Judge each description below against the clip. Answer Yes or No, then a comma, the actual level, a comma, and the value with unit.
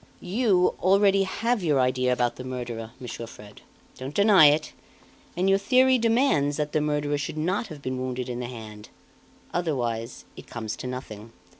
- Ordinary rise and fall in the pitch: No, wide, 7.4 semitones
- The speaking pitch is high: No, medium, 145 Hz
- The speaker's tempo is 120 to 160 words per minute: No, average, 170 wpm